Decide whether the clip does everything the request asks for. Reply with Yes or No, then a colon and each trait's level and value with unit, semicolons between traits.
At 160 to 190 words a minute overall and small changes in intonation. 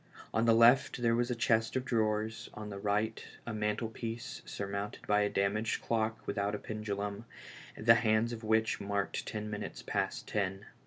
Yes: average, 170 wpm; narrow, 1.8 semitones